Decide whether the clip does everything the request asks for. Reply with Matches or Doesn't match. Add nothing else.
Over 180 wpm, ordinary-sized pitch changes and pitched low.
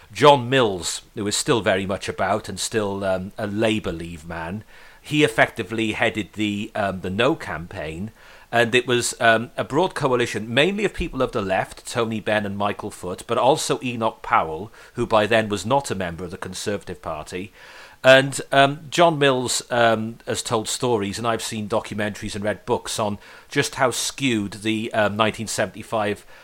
Doesn't match